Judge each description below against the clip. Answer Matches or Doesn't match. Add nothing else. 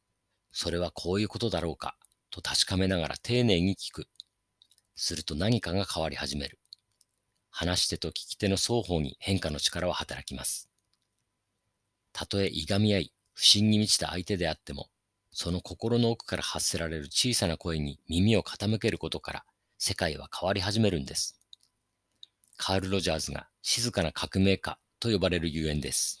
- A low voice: Matches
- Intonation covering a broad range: Doesn't match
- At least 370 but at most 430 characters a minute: Doesn't match